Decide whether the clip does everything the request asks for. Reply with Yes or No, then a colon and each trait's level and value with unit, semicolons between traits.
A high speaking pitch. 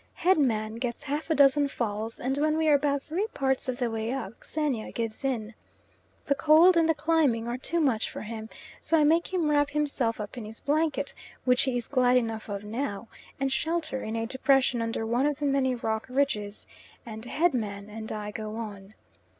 Yes: very high, 255 Hz